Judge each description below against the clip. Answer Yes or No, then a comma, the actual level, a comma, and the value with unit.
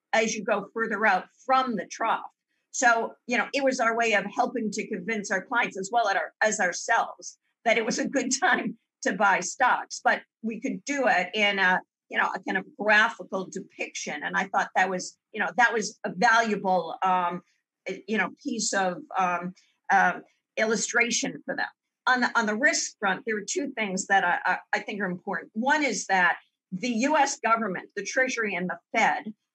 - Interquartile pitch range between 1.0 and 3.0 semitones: No, average, 3.8 semitones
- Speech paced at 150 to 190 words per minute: No, average, 200 wpm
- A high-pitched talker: Yes, high, 225 Hz